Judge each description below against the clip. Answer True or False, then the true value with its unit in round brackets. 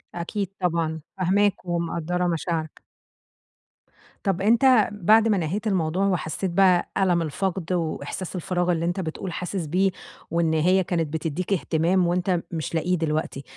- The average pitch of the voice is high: False (175 Hz)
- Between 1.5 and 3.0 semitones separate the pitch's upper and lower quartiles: True (2.6 semitones)